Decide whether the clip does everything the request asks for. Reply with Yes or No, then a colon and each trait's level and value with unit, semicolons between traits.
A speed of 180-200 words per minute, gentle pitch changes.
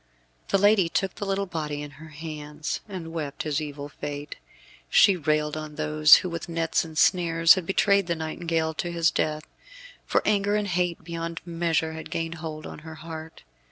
Yes: average, 185 wpm; narrow, 2.1 semitones